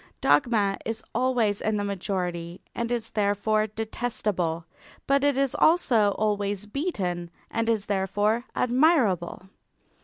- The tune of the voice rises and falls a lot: No, average, 3.4 semitones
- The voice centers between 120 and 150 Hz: No, high, 210 Hz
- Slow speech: Yes, slow, 120 wpm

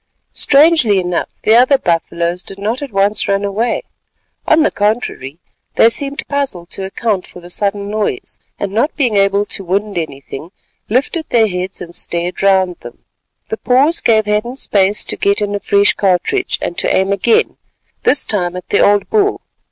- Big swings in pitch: No, average, 4.2 semitones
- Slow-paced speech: No, average, 175 wpm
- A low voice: No, high, 205 Hz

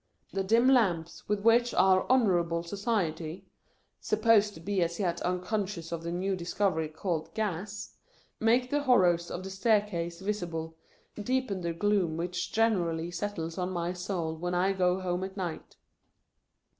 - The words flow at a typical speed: Yes, average, 150 wpm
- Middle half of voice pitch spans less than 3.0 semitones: No, average, 3.5 semitones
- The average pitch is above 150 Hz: Yes, medium, 185 Hz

